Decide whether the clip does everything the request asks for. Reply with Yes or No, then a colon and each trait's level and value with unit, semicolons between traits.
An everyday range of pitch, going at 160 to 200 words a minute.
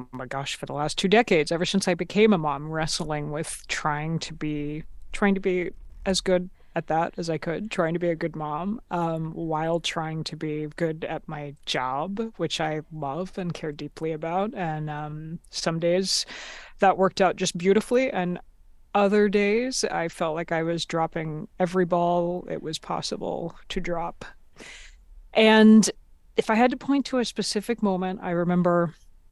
Yes: average, 3.6 semitones; average, 180 wpm